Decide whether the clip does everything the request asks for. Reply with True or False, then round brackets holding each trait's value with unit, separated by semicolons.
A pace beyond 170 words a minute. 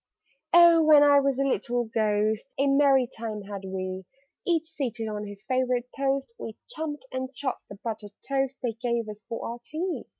True (180 wpm)